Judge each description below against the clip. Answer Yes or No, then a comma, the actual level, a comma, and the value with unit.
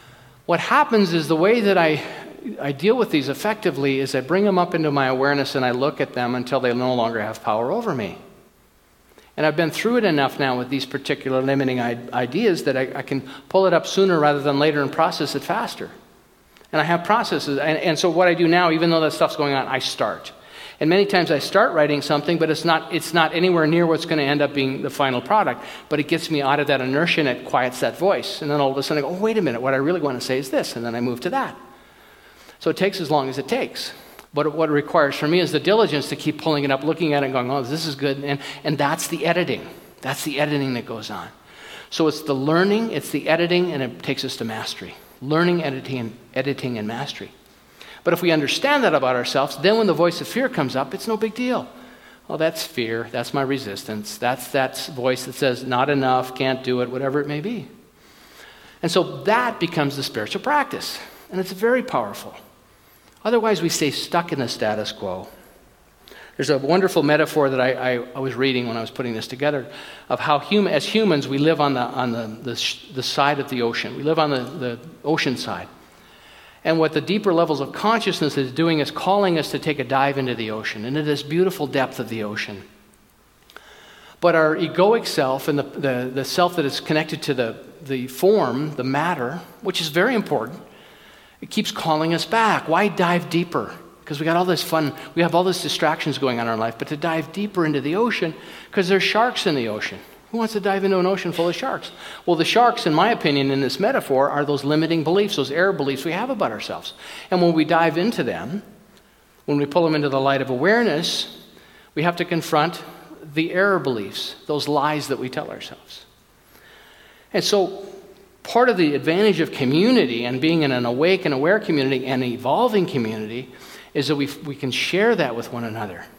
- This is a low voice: No, medium, 150 Hz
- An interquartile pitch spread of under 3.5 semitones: No, average, 4.5 semitones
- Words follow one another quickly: Yes, fast, 225 wpm